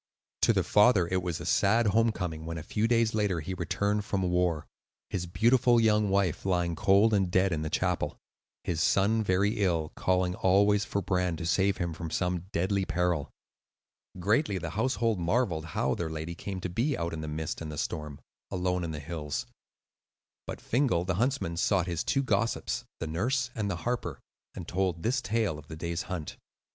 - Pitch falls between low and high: No, very low, 90 Hz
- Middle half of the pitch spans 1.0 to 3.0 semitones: No, average, 3.9 semitones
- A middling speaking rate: Yes, average, 190 wpm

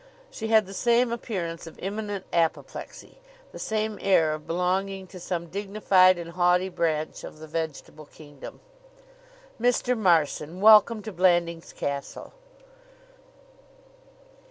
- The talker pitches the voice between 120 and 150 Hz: No, medium, 185 Hz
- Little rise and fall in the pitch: No, average, 4.0 semitones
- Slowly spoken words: Yes, slow, 120 wpm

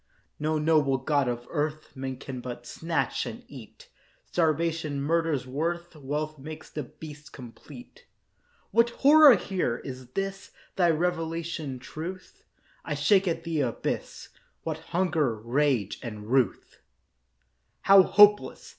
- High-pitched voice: No, medium, 155 Hz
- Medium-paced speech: No, slow, 125 wpm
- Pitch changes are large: No, average, 4.6 semitones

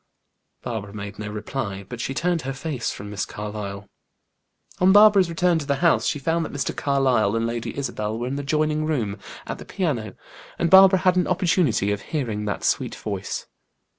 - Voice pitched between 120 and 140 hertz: Yes, low, 135 Hz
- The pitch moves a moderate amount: No, wide, 7.7 semitones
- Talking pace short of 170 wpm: No, average, 190 wpm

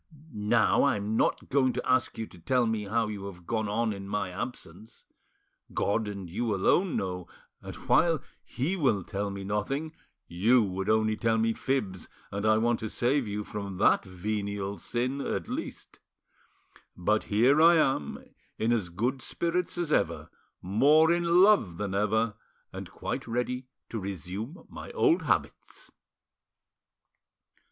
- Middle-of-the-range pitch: No, low, 110 Hz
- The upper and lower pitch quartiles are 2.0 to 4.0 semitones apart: No, average, 4.5 semitones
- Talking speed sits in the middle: Yes, average, 155 wpm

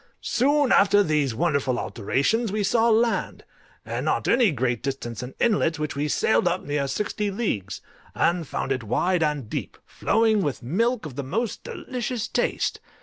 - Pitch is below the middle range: No, medium, 170 Hz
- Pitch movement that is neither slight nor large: No, wide, 8.5 semitones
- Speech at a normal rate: Yes, average, 170 wpm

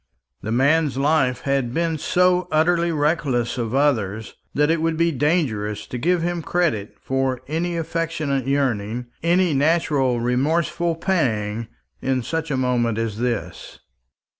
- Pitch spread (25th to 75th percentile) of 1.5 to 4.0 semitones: No, average, 5.2 semitones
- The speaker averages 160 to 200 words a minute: No, average, 140 wpm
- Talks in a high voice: No, medium, 140 Hz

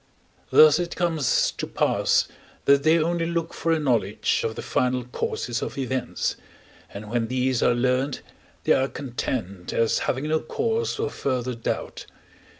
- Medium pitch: No, low, 130 Hz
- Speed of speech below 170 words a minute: Yes, average, 155 wpm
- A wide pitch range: No, average, 4.8 semitones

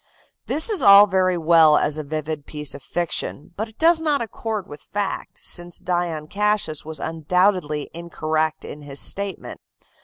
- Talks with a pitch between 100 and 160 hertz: No, medium, 170 Hz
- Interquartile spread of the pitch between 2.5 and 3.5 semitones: No, average, 4.6 semitones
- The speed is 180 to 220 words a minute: No, average, 160 wpm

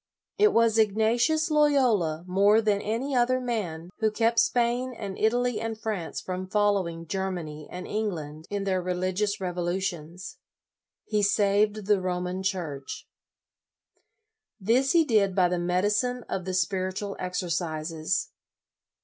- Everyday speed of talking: No, slow, 130 wpm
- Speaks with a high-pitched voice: Yes, high, 200 Hz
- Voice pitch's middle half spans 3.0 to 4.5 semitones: Yes, average, 3.7 semitones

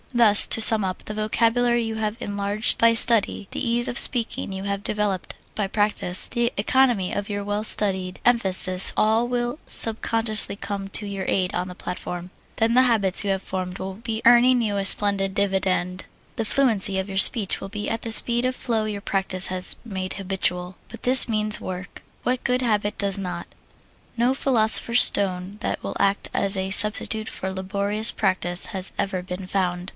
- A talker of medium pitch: No, high, 205 Hz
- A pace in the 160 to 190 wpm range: Yes, average, 185 wpm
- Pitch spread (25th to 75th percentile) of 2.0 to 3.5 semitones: Yes, average, 3.1 semitones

